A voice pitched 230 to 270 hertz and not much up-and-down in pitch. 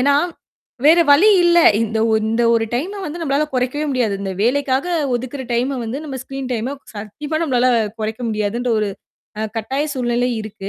No: very high, 255 Hz; average, 4.1 semitones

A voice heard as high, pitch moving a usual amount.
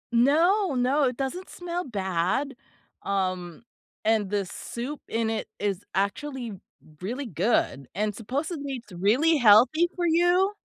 No: high, 245 Hz; wide, 6.8 semitones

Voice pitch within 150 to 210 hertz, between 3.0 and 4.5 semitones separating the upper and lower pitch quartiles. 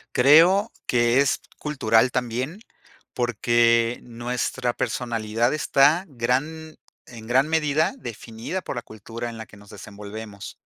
No: low, 120 Hz; average, 3.6 semitones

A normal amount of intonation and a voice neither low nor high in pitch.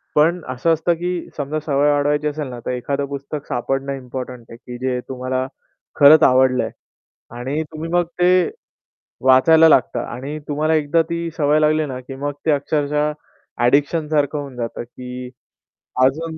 Yes: average, 3.1 semitones; medium, 145 Hz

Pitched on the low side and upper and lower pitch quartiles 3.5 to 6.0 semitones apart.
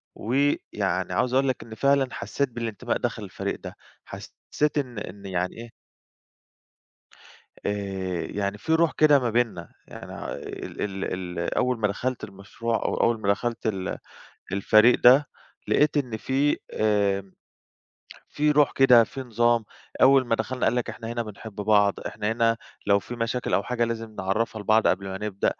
Yes: low, 115 Hz; average, 3.8 semitones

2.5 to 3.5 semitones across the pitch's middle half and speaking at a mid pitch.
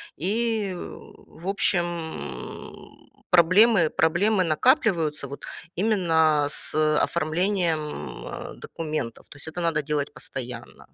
No: average, 3.9 semitones; medium, 165 Hz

